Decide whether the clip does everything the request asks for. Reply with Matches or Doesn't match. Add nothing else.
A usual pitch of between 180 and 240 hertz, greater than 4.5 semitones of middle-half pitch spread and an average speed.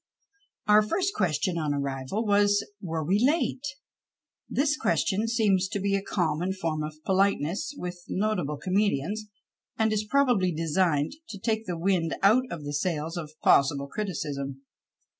Matches